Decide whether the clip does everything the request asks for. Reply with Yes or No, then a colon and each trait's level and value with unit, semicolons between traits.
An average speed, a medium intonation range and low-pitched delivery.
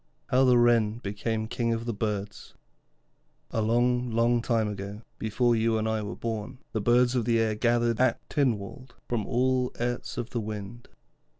No: average, 175 wpm; narrow, 1.9 semitones; low, 115 Hz